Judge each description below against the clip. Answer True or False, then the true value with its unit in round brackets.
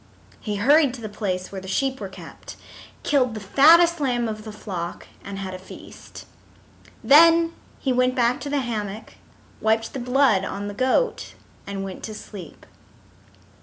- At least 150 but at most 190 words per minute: True (165 wpm)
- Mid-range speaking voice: False (225 Hz)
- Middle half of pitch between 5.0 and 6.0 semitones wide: True (5.3 semitones)